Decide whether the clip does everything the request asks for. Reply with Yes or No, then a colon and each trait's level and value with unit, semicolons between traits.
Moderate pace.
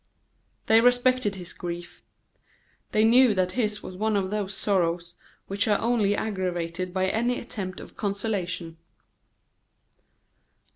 No: slow, 125 wpm